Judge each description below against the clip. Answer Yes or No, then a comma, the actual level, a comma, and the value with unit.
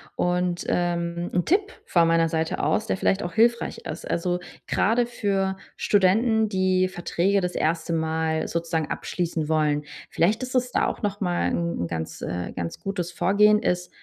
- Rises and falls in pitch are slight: No, average, 3.5 semitones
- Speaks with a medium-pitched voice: Yes, medium, 175 Hz